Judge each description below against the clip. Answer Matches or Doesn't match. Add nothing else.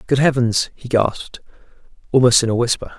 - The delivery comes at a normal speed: Matches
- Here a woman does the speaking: Doesn't match